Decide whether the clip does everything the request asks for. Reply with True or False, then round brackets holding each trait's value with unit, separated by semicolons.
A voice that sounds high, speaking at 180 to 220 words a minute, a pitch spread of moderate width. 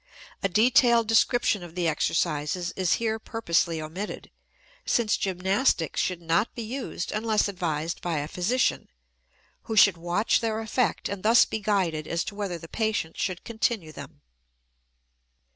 False (195 Hz; 145 wpm; 4.7 semitones)